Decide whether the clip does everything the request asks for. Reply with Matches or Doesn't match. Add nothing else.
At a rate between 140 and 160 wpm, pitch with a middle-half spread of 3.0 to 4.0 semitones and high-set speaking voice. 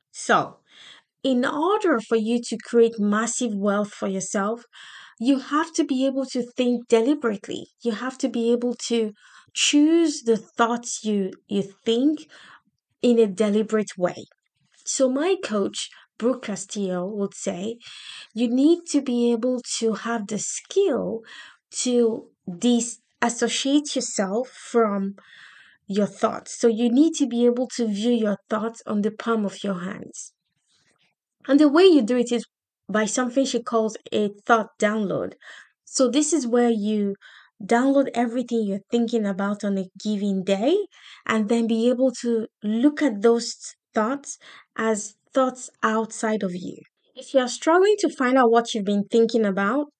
Matches